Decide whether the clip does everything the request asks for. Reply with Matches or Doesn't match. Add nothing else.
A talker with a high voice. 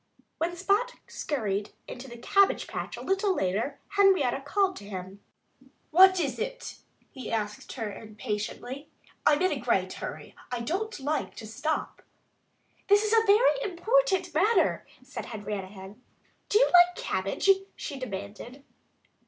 Matches